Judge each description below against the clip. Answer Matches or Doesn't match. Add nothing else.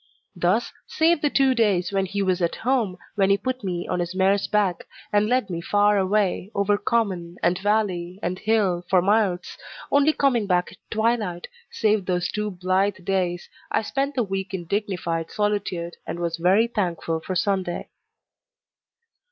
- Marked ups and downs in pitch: Doesn't match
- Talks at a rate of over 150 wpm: Matches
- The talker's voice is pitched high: Matches